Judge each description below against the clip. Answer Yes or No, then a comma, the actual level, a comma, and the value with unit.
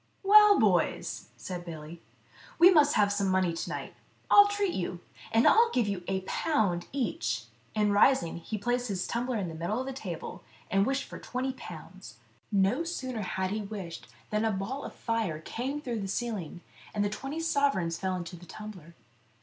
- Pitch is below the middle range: No, high, 210 Hz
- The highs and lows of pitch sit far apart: Yes, wide, 6.3 semitones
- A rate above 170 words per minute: Yes, average, 180 wpm